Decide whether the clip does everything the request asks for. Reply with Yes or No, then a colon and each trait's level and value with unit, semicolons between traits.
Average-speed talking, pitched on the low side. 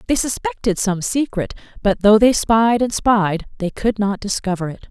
No: average, 185 wpm; high, 215 Hz